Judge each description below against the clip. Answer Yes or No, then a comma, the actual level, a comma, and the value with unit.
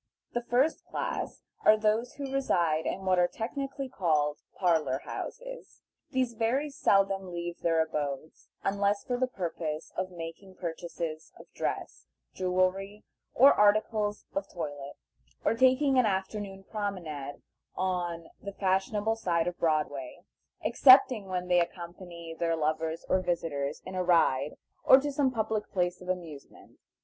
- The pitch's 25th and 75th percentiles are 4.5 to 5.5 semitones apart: Yes, average, 4.9 semitones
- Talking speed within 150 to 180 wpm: No, average, 140 wpm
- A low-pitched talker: No, medium, 185 Hz